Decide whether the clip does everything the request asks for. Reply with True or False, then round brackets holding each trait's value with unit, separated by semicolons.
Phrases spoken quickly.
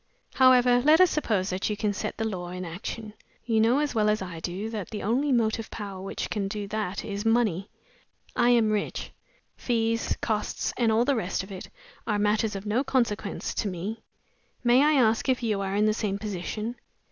True (210 wpm)